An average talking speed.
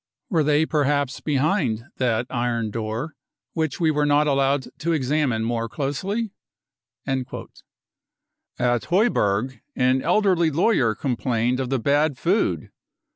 No: slow, 130 wpm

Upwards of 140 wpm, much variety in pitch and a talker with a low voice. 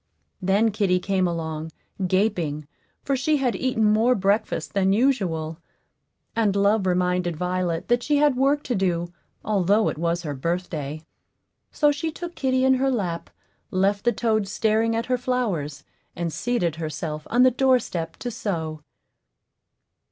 No: average, 150 wpm; wide, 6.1 semitones; high, 200 Hz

